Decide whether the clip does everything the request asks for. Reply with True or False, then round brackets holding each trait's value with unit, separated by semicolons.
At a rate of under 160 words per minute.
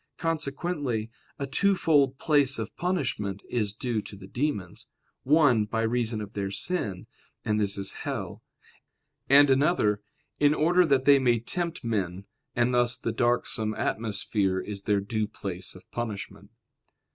True (145 wpm)